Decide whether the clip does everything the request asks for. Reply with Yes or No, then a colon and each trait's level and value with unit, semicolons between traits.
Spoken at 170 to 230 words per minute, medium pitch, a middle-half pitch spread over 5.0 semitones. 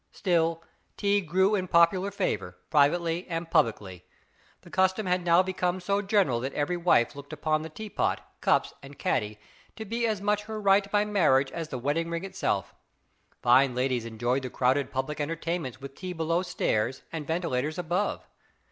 Yes: average, 175 wpm; medium, 165 Hz; wide, 5.5 semitones